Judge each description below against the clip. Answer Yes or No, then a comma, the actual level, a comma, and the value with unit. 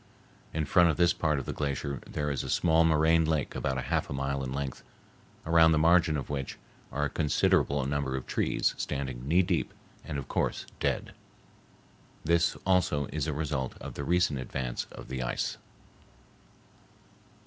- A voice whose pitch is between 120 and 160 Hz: No, very low, 75 Hz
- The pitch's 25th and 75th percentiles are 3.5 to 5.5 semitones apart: No, average, 3.1 semitones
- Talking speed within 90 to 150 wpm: No, average, 170 wpm